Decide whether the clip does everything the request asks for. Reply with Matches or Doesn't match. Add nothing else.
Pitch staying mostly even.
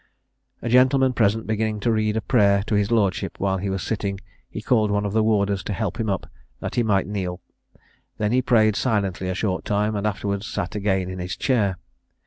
Matches